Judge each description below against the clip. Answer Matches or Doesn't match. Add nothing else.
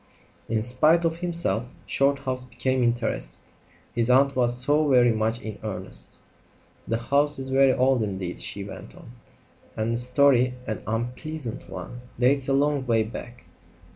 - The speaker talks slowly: Doesn't match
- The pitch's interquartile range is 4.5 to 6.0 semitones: Doesn't match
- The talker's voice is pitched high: Doesn't match